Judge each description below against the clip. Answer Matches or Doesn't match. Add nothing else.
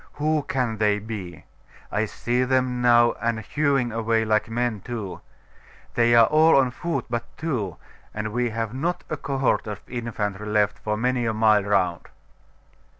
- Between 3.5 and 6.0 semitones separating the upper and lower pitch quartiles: Doesn't match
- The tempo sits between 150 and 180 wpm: Matches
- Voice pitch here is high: Doesn't match